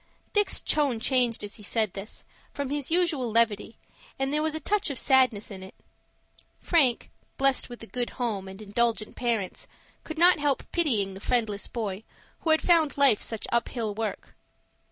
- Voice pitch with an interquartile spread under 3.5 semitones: No, average, 5.2 semitones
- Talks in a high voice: Yes, high, 240 Hz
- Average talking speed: Yes, average, 175 wpm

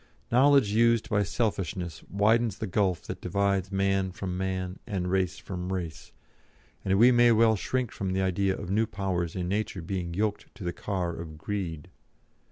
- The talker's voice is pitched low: Yes, very low, 95 Hz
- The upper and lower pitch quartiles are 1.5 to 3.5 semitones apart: Yes, average, 2.7 semitones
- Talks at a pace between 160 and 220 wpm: Yes, average, 175 wpm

